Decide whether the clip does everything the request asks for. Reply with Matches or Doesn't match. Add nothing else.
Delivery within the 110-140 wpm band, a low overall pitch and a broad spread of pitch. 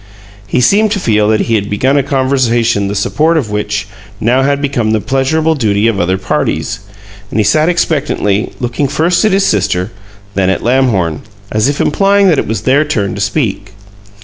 Doesn't match